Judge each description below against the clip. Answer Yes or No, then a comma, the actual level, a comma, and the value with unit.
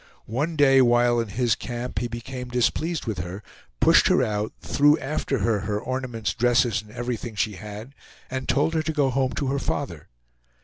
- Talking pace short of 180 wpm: No, average, 185 wpm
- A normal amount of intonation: Yes, average, 3.7 semitones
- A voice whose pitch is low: Yes, low, 120 Hz